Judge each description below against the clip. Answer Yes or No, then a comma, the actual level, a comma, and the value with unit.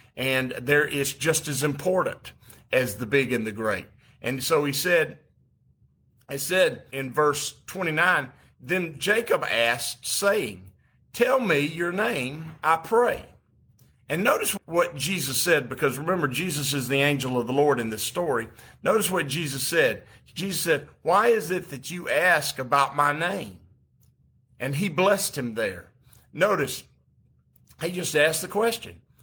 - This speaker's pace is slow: No, average, 150 wpm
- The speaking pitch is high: No, medium, 145 Hz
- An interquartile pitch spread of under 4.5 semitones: No, wide, 5.5 semitones